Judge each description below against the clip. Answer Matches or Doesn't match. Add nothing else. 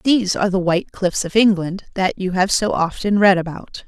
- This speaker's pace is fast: Matches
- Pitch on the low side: Doesn't match